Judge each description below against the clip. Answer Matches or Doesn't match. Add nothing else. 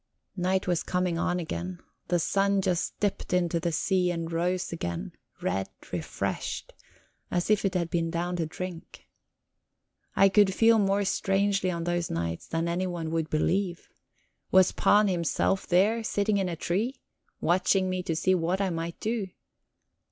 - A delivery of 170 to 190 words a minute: Doesn't match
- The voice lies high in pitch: Doesn't match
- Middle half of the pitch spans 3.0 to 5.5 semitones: Doesn't match